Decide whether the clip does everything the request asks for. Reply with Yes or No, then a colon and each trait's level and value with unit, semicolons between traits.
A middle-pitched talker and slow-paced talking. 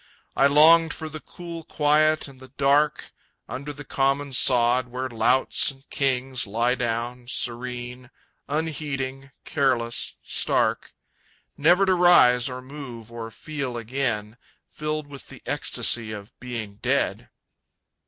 No: low, 130 Hz; slow, 125 wpm